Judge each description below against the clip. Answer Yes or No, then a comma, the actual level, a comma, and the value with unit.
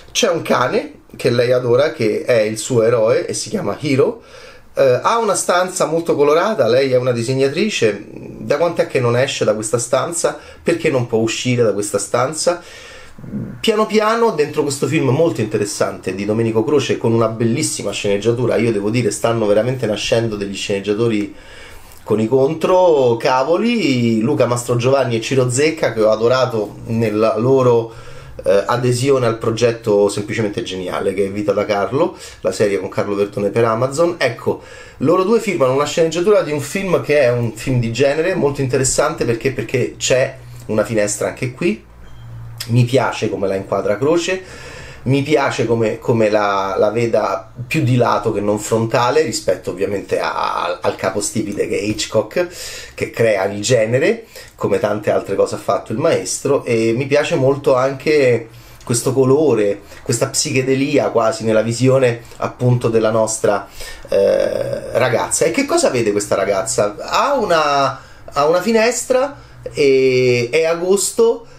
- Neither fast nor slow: Yes, average, 160 wpm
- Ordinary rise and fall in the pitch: No, wide, 6.0 semitones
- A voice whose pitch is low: Yes, low, 125 Hz